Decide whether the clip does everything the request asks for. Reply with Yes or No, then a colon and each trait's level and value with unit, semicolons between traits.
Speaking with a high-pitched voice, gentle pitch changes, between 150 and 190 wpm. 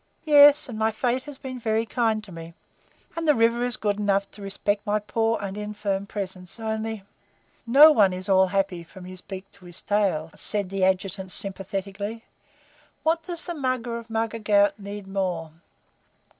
No: high, 210 Hz; average, 3.0 semitones; average, 180 wpm